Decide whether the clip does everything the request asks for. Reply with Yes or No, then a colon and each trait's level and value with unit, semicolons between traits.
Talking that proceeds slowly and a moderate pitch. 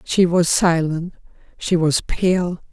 Yes: slow, 130 wpm; medium, 170 Hz